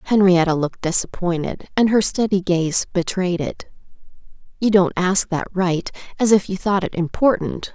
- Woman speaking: Yes, female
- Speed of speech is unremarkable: Yes, average, 145 wpm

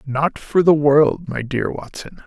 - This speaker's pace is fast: No, average, 185 wpm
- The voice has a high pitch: No, medium, 145 Hz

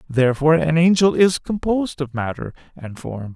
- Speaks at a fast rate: No, average, 160 wpm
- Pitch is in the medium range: Yes, medium, 150 Hz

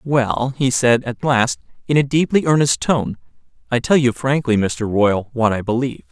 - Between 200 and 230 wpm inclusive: No, average, 185 wpm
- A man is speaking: Yes, male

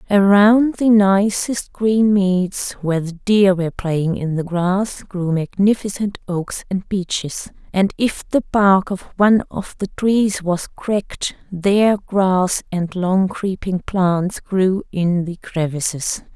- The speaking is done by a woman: Yes, female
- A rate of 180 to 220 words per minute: No, average, 145 wpm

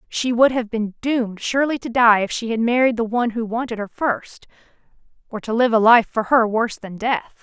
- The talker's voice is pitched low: No, high, 230 Hz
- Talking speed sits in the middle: No, fast, 220 wpm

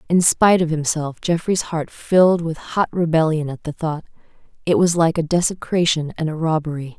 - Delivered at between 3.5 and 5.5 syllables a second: Yes, 5.2 syllables/s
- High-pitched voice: No, medium, 160 Hz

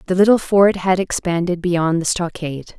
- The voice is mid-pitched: Yes, medium, 180 Hz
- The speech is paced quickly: No, average, 170 wpm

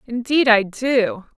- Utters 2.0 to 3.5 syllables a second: Yes, 3.4 syllables/s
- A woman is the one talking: Yes, female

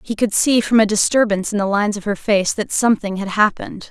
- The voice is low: No, high, 210 Hz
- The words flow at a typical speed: No, fast, 245 wpm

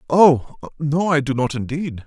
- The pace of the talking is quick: No, average, 175 wpm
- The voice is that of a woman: No, male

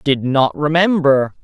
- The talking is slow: Yes, slow, 125 wpm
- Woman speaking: No, male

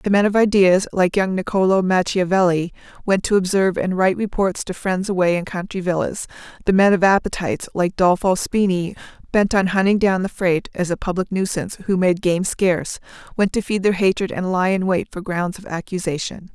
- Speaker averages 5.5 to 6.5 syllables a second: Yes, 5.6 syllables/s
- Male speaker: No, female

